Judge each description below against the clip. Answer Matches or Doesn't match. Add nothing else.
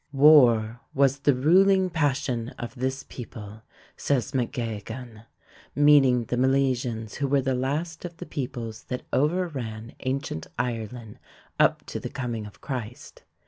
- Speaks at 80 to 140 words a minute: Matches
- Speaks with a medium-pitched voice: Doesn't match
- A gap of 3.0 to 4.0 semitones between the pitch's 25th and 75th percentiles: Matches